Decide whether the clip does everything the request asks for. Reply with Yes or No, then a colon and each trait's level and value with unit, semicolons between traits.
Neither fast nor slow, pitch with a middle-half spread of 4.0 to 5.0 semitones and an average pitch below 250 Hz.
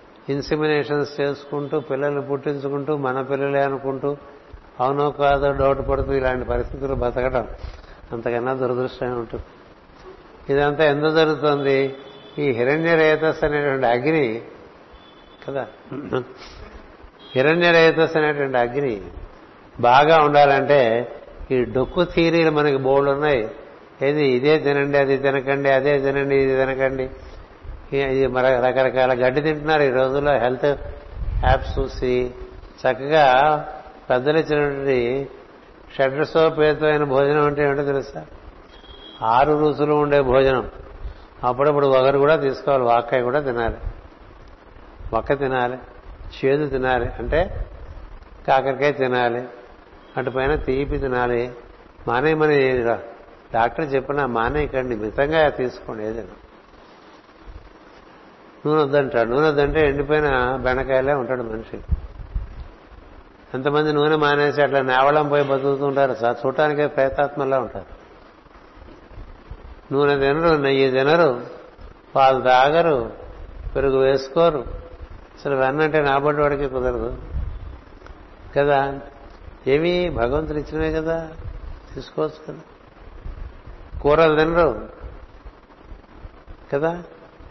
No: average, 90 wpm; average, 3.0 semitones; low, 135 Hz